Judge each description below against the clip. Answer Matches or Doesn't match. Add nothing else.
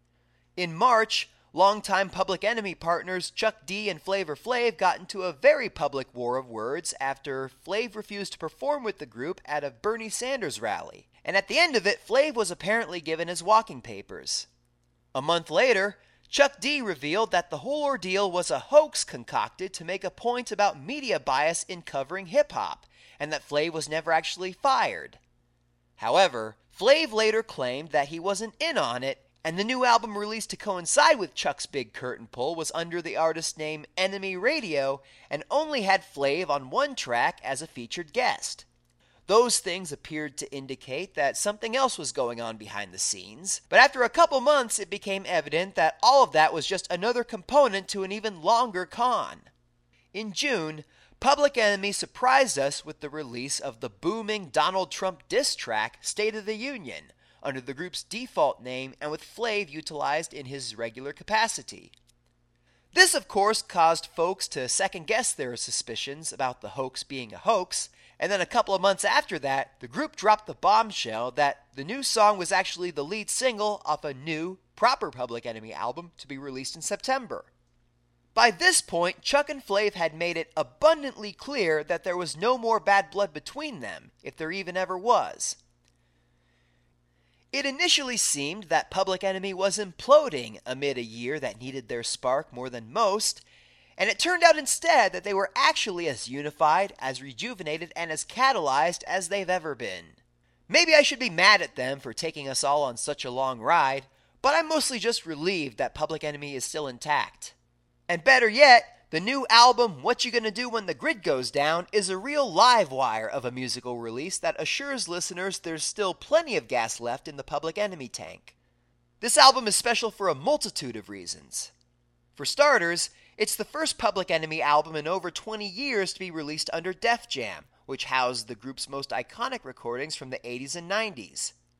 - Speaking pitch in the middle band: Matches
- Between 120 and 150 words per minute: Doesn't match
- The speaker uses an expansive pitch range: Matches